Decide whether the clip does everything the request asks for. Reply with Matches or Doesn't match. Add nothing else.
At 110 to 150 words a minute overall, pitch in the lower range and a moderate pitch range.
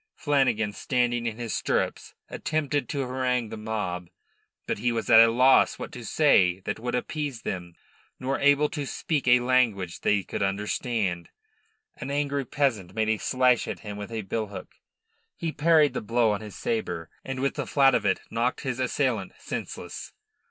Doesn't match